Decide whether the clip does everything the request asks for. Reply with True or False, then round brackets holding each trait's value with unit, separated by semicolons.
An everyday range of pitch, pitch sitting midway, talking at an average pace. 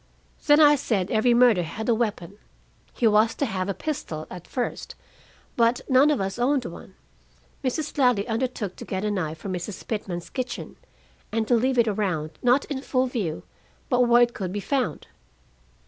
False (4.7 semitones; 225 Hz; 180 wpm)